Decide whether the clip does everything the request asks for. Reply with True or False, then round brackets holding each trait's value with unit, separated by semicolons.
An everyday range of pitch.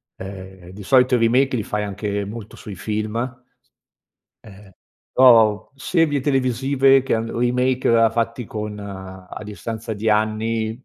True (3.3 semitones)